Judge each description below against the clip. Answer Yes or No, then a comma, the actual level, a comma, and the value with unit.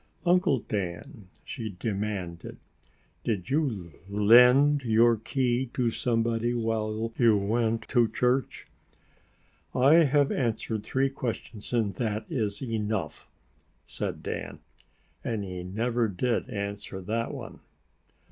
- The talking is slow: Yes, slow, 110 wpm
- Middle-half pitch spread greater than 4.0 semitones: No, average, 3.1 semitones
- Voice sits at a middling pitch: No, low, 115 Hz